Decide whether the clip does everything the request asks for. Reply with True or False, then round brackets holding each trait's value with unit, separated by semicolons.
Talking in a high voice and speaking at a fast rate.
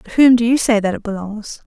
True (220 Hz; 280 wpm)